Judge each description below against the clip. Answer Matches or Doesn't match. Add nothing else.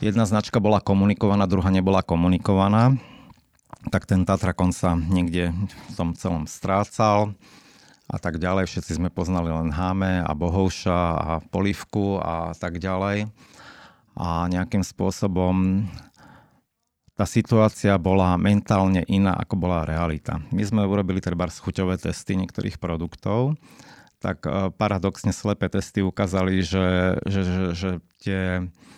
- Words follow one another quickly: Doesn't match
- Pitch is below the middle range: Matches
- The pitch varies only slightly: Matches